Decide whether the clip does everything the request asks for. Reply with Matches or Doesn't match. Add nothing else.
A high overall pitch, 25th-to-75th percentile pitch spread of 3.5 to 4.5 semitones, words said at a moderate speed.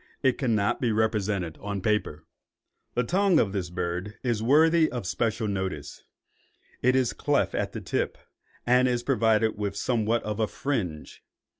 Doesn't match